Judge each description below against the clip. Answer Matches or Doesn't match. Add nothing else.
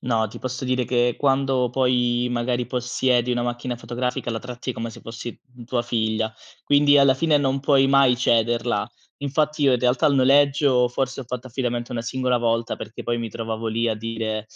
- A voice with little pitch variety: Matches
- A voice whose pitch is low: Matches